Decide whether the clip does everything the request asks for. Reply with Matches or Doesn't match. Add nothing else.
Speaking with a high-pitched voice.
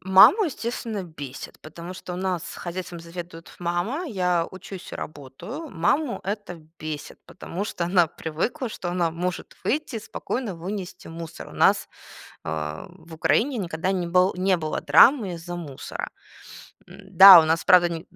Doesn't match